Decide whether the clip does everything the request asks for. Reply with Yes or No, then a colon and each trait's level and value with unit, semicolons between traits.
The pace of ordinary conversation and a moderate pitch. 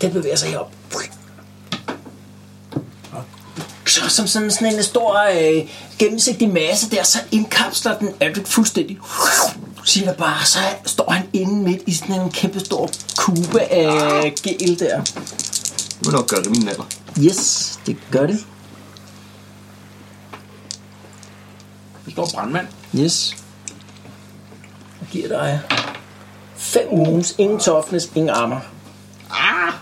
No: slow, 125 wpm; medium, 150 Hz